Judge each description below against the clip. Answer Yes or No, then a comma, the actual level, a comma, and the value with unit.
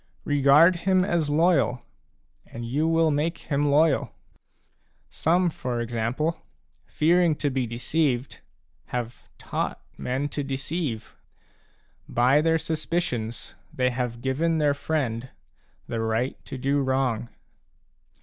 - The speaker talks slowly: Yes, slow, 115 wpm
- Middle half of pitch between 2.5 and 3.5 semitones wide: No, average, 4.7 semitones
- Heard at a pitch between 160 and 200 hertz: No, medium, 140 Hz